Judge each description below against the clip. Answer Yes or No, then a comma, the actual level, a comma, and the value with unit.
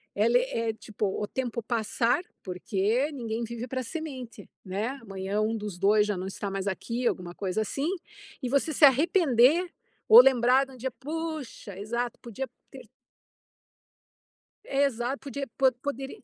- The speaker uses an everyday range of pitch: Yes, average, 4.4 semitones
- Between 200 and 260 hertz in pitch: Yes, high, 240 Hz